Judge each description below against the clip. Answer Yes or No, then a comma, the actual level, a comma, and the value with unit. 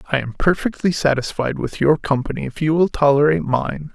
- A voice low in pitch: No, medium, 150 Hz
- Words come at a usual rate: Yes, average, 185 wpm